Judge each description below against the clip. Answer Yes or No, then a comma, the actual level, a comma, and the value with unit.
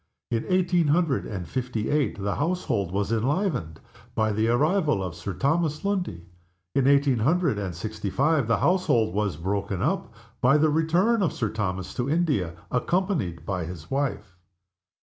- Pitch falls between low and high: No, low, 120 Hz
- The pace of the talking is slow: No, average, 160 wpm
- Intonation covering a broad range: Yes, wide, 8.2 semitones